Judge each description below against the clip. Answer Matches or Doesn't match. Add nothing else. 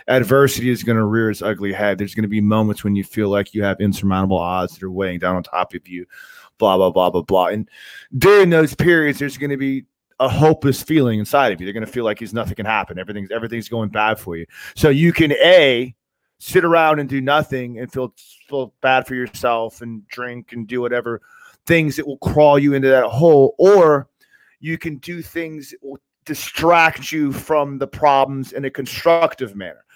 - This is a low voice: Matches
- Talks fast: Matches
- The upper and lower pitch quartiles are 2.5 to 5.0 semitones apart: Doesn't match